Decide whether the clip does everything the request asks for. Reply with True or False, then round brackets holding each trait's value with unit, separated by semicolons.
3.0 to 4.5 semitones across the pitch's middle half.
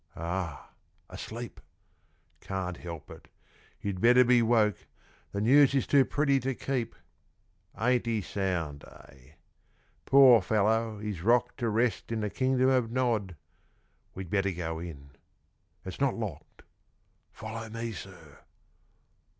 False (4.9 semitones)